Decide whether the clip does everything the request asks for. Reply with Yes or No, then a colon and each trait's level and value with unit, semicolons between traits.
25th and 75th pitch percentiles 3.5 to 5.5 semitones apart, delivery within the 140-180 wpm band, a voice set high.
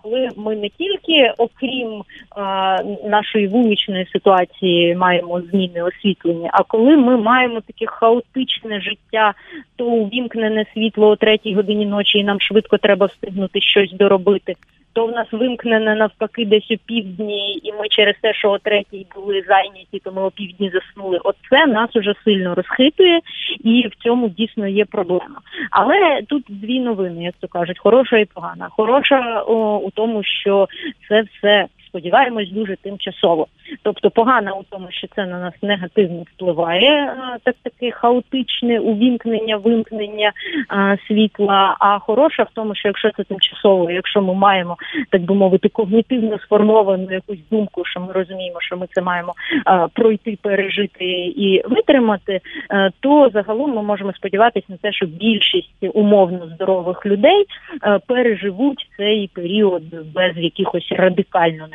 No: average, 2.9 semitones; average, 145 wpm; high, 210 Hz